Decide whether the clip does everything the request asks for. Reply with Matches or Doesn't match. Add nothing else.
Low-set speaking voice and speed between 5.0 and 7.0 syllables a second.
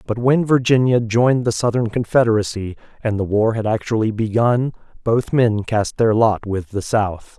Doesn't match